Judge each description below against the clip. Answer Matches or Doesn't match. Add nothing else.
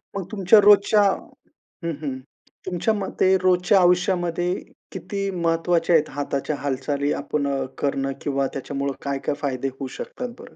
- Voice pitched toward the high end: Doesn't match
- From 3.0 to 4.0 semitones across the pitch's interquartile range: Doesn't match